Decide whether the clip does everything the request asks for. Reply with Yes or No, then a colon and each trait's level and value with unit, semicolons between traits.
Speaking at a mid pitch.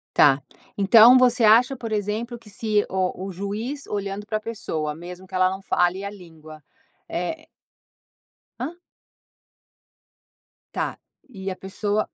No: high, 205 Hz